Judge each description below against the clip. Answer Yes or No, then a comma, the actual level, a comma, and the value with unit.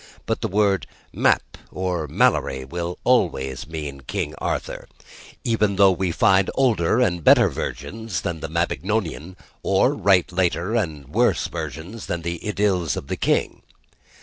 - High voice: No, very low, 90 Hz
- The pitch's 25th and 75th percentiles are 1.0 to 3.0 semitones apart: No, average, 4.0 semitones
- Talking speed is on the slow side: No, average, 145 wpm